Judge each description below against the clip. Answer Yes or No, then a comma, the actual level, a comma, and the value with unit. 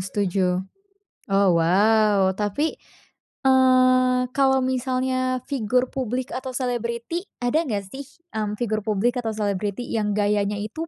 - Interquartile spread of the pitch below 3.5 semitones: No, average, 3.8 semitones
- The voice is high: Yes, high, 230 Hz